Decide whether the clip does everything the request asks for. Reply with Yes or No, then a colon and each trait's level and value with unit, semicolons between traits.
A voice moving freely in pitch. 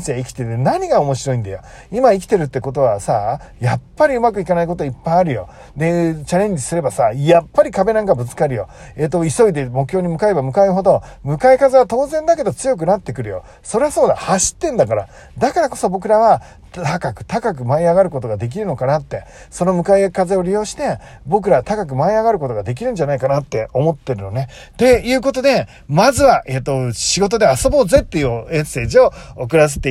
Yes: wide, 7.6 semitones